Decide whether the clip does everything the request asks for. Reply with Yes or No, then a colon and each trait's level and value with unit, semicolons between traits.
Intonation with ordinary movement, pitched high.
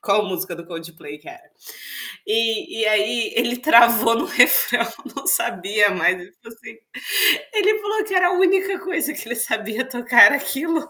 No: wide, 8.0 semitones; high, 235 Hz